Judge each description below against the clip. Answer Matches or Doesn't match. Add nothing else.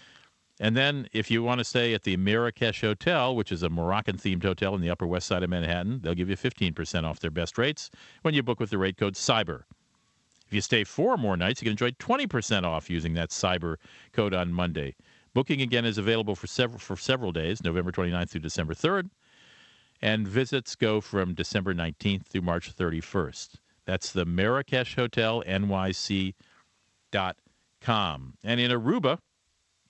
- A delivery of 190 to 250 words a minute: Doesn't match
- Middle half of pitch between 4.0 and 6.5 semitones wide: Matches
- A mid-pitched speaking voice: Doesn't match